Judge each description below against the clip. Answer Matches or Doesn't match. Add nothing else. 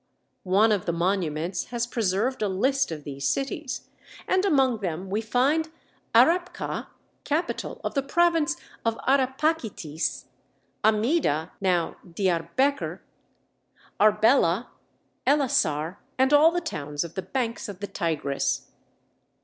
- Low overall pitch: Doesn't match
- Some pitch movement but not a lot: Doesn't match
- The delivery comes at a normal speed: Doesn't match